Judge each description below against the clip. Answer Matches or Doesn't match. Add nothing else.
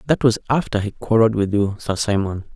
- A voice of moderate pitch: Doesn't match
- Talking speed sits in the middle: Doesn't match